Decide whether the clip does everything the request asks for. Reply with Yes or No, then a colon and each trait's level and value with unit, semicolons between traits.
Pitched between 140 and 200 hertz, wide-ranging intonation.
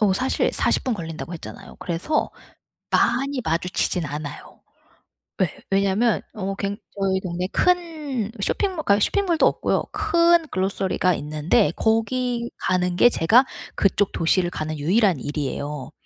Yes: high, 195 Hz; wide, 6.9 semitones